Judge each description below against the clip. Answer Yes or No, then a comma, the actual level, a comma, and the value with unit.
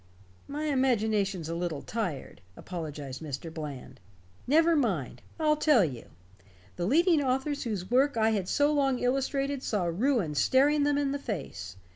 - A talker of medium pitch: No, high, 230 Hz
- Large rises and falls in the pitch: Yes, wide, 9.0 semitones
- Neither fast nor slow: Yes, average, 150 wpm